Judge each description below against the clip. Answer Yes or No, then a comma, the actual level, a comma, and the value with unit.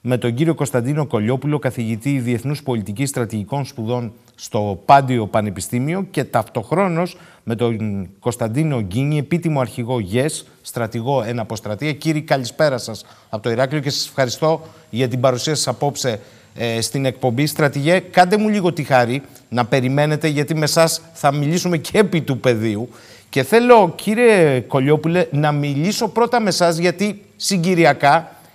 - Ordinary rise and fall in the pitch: Yes, average, 4.8 semitones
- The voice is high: No, medium, 140 Hz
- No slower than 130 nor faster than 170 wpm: Yes, average, 145 wpm